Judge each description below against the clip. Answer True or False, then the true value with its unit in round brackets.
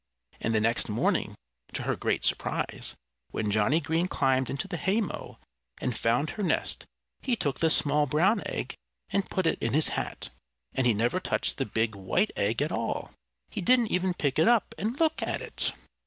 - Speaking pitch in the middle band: True (150 Hz)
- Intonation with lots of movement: True (8.3 semitones)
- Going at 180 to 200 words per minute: True (190 wpm)